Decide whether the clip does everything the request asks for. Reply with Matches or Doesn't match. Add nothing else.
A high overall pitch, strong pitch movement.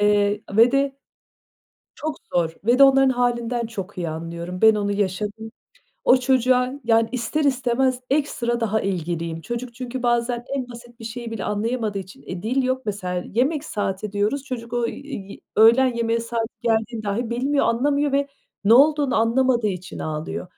Doesn't match